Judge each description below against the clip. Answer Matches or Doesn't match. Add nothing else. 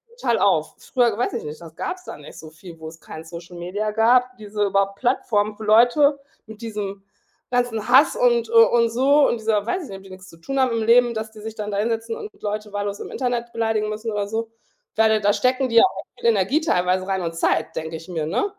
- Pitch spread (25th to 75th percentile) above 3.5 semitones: Matches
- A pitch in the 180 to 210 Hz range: Doesn't match